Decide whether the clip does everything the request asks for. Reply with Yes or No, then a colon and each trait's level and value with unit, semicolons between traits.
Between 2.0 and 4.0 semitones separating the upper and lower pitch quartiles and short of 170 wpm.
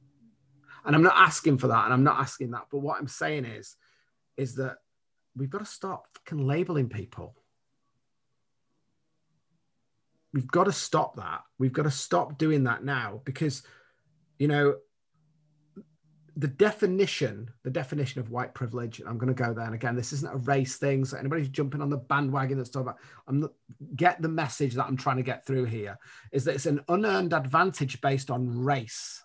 No: average, 3.3 semitones; average, 180 wpm